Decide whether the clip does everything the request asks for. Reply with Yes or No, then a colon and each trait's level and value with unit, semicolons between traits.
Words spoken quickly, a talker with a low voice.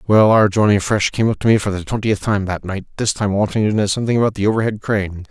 Yes: fast, 270 wpm; low, 105 Hz